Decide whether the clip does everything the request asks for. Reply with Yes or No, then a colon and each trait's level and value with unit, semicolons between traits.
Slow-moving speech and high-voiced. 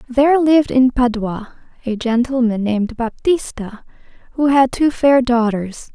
Yes: slow, 130 wpm; high, 245 Hz